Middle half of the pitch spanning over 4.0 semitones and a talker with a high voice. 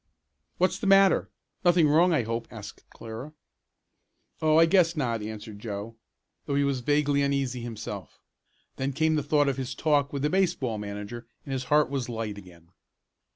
No: average, 5.0 semitones; medium, 140 Hz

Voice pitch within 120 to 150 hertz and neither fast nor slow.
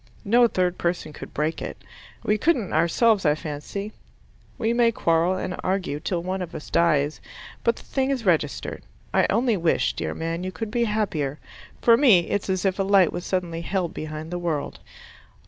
No: medium, 185 Hz; average, 185 wpm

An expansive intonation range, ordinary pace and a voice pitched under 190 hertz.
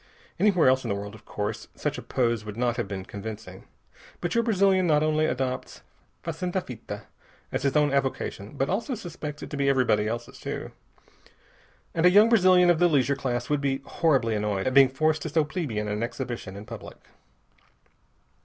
Yes: wide, 6.4 semitones; average, 190 wpm; low, 135 Hz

